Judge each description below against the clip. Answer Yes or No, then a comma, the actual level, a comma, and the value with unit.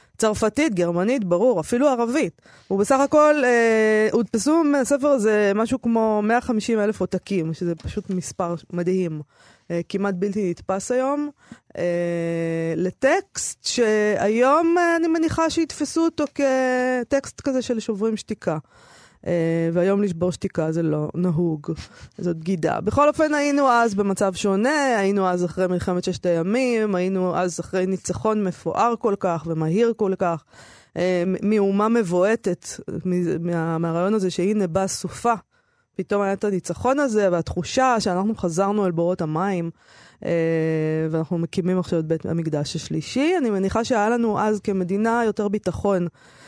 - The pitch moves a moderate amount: Yes, average, 5.0 semitones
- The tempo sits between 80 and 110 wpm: No, average, 130 wpm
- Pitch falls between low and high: No, high, 200 Hz